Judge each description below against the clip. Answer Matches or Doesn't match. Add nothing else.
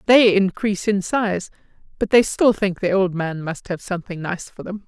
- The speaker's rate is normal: Doesn't match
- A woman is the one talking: Matches